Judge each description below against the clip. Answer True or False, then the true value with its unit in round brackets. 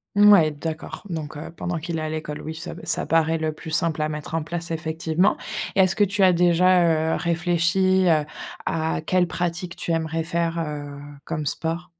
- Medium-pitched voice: True (165 Hz)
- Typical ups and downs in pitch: False (2.0 semitones)